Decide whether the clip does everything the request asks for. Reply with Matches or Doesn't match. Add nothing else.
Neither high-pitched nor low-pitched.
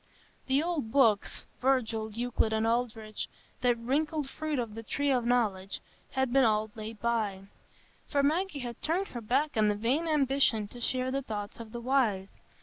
Doesn't match